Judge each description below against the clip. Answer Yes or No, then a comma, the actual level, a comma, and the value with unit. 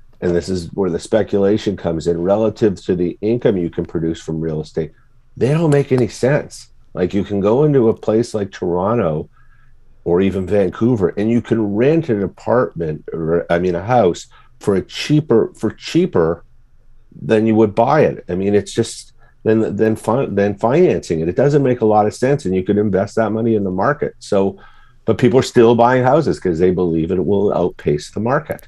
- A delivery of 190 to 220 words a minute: Yes, average, 200 wpm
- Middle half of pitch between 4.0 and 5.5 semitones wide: Yes, average, 4.7 semitones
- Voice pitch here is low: Yes, low, 110 Hz